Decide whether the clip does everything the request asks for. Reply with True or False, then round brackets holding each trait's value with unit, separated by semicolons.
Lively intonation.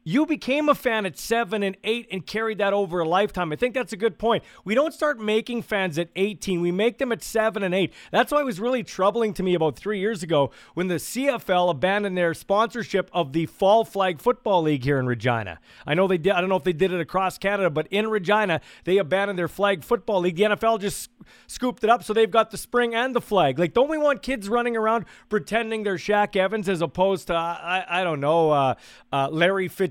False (4.1 semitones)